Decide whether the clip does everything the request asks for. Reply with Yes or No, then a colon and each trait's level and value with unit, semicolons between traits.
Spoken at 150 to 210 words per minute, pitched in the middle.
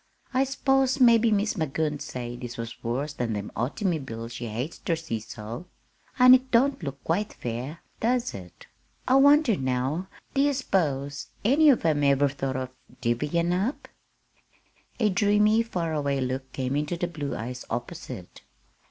Yes: average, 160 wpm; medium, 150 Hz